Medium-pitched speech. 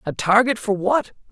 No: high, 215 Hz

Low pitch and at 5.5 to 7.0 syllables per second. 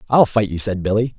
Yes: low, 105 Hz; 6.0 syllables/s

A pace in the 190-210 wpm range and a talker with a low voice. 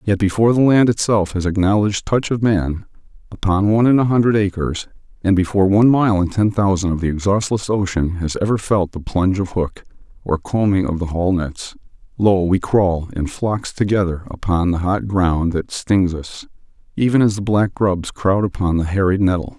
Yes: average, 195 wpm; very low, 95 Hz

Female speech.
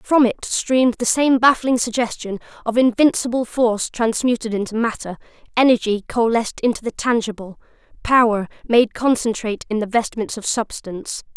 Yes: female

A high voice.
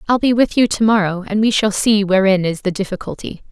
Yes: high, 205 Hz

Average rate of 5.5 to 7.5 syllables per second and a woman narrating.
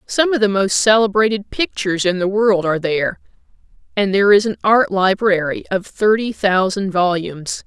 No: 5.2 syllables/s; female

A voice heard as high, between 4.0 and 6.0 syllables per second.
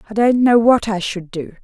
Yes: high, 215 Hz; 5.0 syllables/s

